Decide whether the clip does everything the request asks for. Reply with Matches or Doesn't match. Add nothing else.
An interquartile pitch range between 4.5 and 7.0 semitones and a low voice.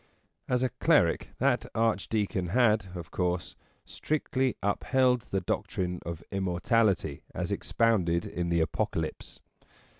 Matches